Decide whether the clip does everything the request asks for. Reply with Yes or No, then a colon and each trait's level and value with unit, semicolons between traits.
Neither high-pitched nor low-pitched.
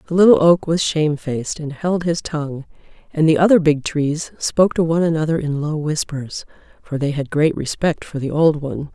Yes: medium, 155 Hz